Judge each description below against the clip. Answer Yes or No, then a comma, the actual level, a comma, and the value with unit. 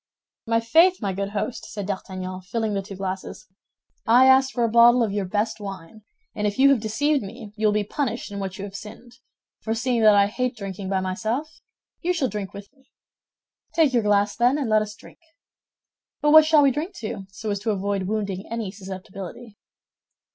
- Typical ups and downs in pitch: Yes, average, 3.8 semitones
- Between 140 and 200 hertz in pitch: No, high, 215 Hz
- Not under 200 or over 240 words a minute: Yes, fast, 205 wpm